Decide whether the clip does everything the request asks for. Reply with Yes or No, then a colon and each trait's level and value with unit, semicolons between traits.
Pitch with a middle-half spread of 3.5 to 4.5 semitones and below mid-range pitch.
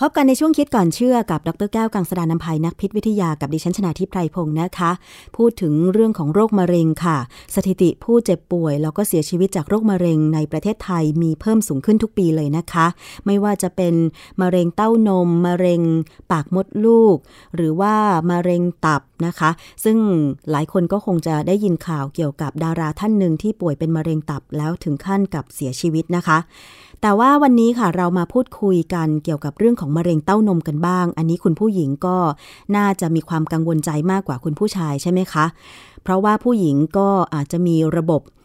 No: average, 3.8 semitones; medium, 175 Hz